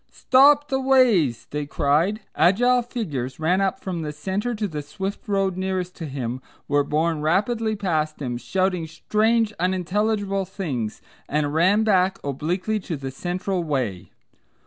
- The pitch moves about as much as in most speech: No, wide, 5.7 semitones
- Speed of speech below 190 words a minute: Yes, average, 145 wpm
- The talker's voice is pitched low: No, medium, 185 Hz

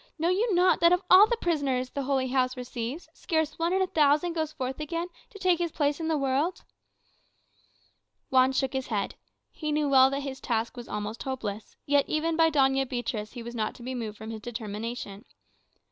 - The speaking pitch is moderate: No, very high, 270 Hz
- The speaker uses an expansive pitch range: No, average, 4.9 semitones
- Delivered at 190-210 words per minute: Yes, fast, 205 wpm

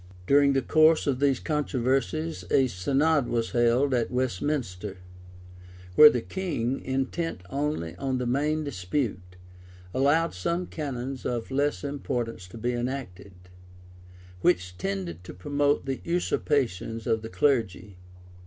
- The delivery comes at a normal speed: No, slow, 125 wpm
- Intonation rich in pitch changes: No, average, 4.4 semitones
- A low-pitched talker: Yes, low, 130 Hz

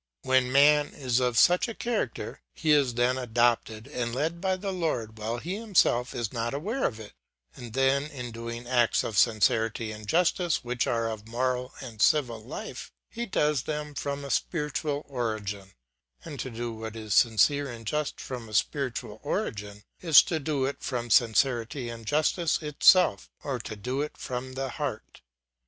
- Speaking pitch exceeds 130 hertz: No, low, 125 Hz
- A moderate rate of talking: Yes, average, 175 wpm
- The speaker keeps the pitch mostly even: No, average, 4.5 semitones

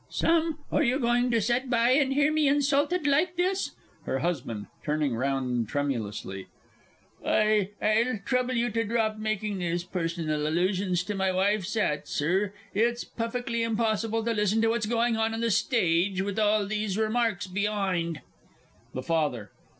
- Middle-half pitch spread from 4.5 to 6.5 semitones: Yes, average, 5.3 semitones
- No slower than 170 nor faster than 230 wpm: No, average, 160 wpm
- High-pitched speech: Yes, high, 215 Hz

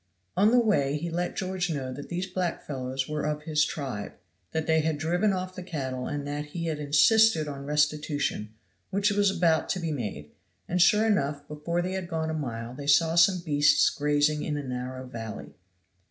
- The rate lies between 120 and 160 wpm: No, average, 195 wpm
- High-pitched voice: No, medium, 150 Hz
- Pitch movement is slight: No, average, 3.8 semitones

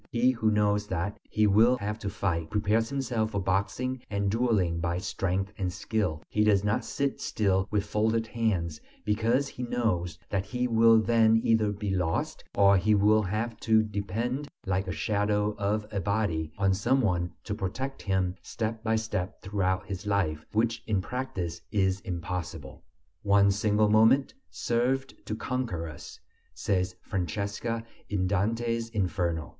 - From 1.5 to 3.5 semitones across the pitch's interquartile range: Yes, average, 3.1 semitones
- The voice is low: Yes, low, 105 Hz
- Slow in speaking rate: No, average, 160 wpm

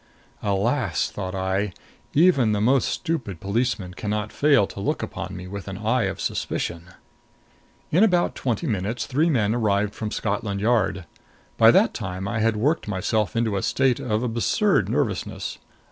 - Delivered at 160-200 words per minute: Yes, average, 165 wpm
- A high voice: No, low, 110 Hz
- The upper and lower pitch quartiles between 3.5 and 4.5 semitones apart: Yes, average, 4.2 semitones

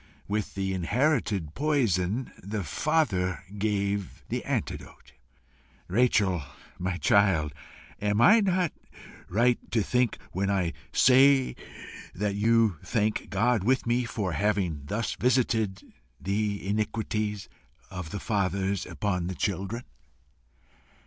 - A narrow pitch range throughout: No, average, 3.6 semitones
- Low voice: Yes, low, 105 Hz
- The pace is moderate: No, slow, 105 wpm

